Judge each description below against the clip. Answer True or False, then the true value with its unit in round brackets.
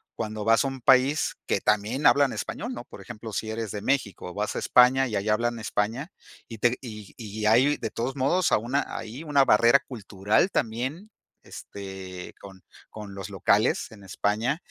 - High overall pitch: False (115 Hz)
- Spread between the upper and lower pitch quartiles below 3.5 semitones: False (4.1 semitones)